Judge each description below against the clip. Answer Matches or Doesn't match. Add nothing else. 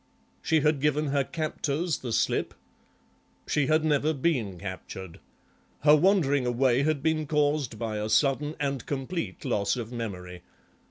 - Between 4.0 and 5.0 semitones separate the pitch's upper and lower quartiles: Matches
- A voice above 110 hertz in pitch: Matches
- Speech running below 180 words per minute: Matches